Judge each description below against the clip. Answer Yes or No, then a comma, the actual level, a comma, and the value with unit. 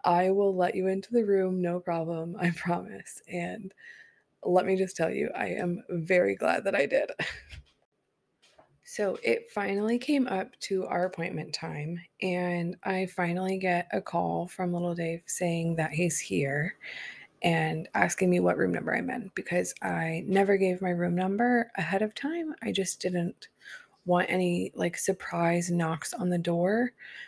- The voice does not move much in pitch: Yes, narrow, 2.0 semitones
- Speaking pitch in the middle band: Yes, medium, 180 Hz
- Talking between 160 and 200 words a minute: Yes, average, 165 wpm